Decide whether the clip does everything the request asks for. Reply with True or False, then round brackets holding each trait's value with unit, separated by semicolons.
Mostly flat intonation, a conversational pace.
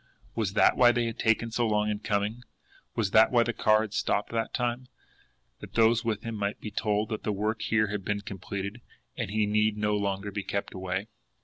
False (1.8 semitones; 215 wpm)